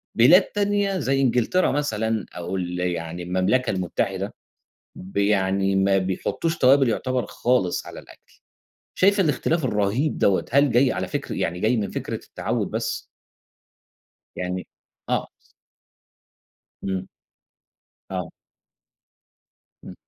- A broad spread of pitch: Yes, wide, 6.5 semitones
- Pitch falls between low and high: No, low, 105 Hz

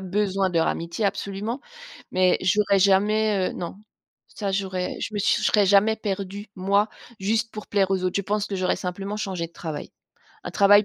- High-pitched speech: Yes, high, 195 Hz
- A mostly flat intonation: Yes, narrow, 1.9 semitones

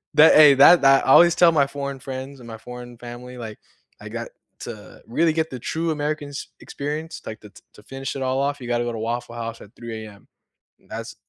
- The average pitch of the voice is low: Yes, low, 130 Hz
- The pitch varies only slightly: No, average, 3.7 semitones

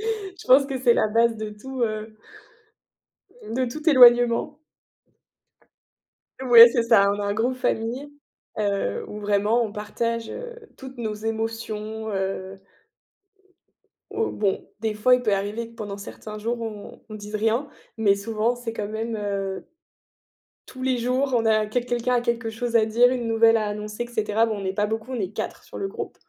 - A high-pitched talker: Yes, high, 225 Hz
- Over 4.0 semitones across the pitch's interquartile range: No, narrow, 2.5 semitones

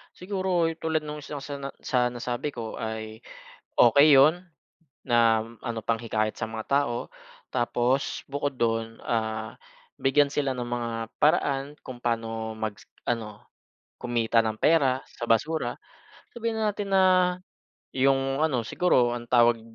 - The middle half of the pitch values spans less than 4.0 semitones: No, average, 4.3 semitones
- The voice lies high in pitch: No, low, 125 Hz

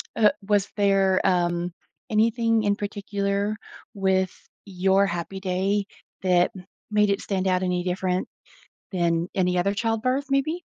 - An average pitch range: No, narrow, 2.2 semitones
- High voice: Yes, high, 195 Hz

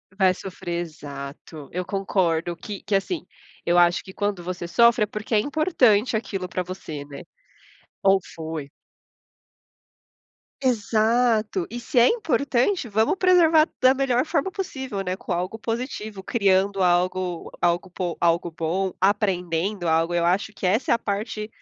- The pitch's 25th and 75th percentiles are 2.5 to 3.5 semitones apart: No, average, 5.0 semitones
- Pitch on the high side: Yes, high, 195 Hz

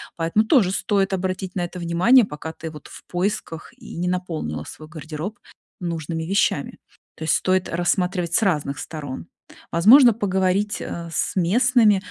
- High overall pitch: No, medium, 180 Hz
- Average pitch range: Yes, average, 3.5 semitones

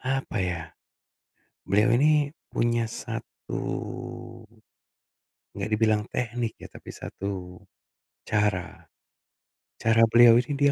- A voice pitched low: Yes, low, 115 Hz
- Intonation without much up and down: No, average, 3.2 semitones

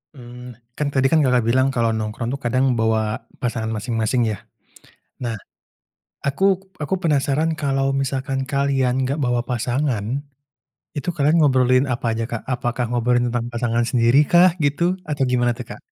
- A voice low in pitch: Yes, low, 125 Hz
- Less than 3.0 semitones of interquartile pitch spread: Yes, narrow, 2.6 semitones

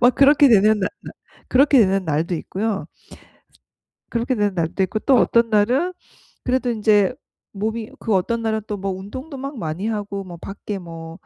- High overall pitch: Yes, high, 215 Hz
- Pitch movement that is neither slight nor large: Yes, average, 4.1 semitones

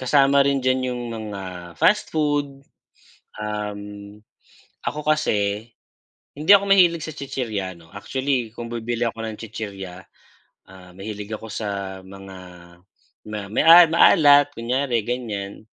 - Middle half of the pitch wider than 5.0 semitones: Yes, wide, 5.5 semitones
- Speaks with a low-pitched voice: Yes, low, 115 Hz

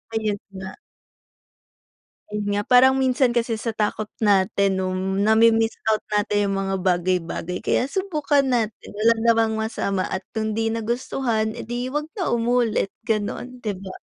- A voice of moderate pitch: No, high, 220 Hz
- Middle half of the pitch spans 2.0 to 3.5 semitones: Yes, average, 3.0 semitones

